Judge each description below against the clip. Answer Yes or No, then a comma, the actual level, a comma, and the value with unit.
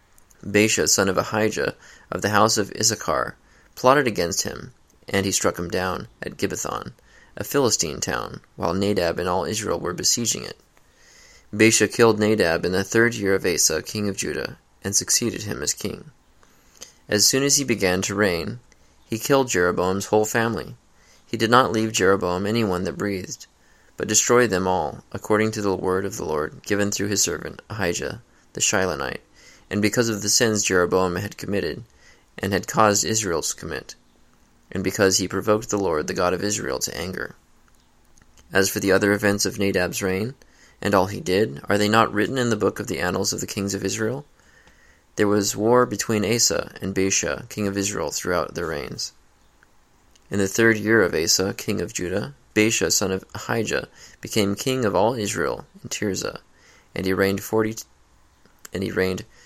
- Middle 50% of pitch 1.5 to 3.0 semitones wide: Yes, narrow, 2.6 semitones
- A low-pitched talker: Yes, low, 100 Hz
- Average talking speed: Yes, average, 180 wpm